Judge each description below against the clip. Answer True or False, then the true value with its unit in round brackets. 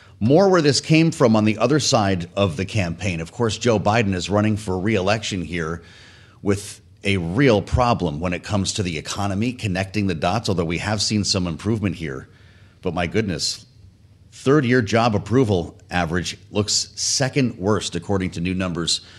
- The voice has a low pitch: True (100 Hz)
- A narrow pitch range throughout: False (3.2 semitones)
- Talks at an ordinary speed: True (180 wpm)